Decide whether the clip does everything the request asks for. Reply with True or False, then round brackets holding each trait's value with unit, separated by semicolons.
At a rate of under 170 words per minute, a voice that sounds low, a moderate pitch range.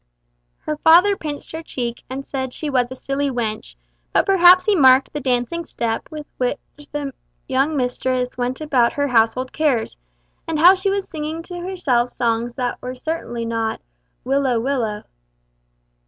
False (160 wpm; 270 Hz; 4.4 semitones)